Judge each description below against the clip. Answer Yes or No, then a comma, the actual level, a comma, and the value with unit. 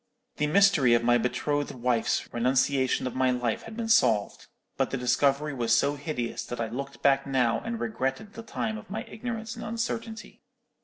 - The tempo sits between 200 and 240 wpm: No, average, 185 wpm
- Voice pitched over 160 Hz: No, medium, 140 Hz